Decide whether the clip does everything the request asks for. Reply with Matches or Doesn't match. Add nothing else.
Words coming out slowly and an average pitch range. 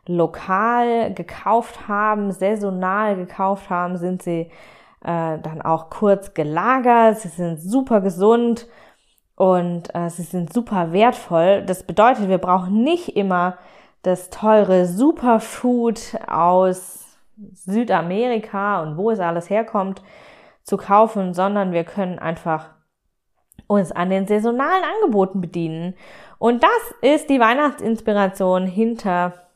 Matches